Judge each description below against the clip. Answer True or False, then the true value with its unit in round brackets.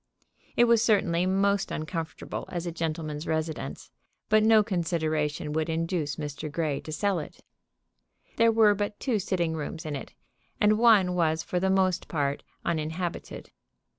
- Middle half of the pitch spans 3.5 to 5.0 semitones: True (4.2 semitones)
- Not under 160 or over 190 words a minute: False (150 wpm)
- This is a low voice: False (170 Hz)